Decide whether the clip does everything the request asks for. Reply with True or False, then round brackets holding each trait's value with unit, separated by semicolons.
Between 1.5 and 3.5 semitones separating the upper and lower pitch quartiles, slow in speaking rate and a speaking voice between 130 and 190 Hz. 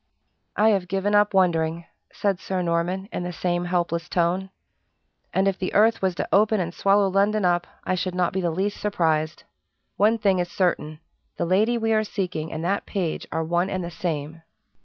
False (2.6 semitones; 195 wpm; 185 Hz)